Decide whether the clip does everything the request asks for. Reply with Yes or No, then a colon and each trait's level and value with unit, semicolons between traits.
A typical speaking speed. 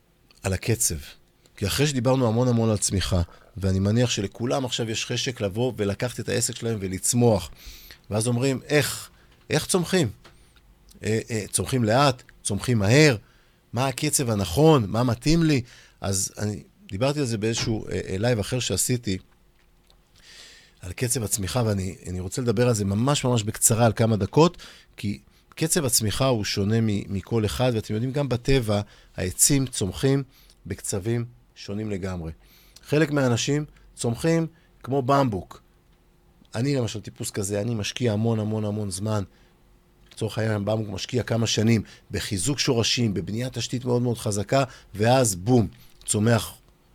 Yes: average, 140 wpm